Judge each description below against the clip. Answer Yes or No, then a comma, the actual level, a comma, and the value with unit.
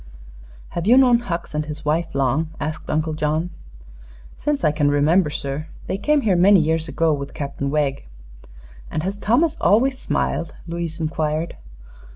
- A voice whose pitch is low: No, medium, 160 Hz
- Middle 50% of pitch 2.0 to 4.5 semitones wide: Yes, average, 4.1 semitones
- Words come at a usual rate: Yes, average, 160 wpm